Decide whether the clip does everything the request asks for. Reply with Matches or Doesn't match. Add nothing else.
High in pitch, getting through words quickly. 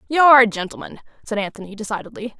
Doesn't match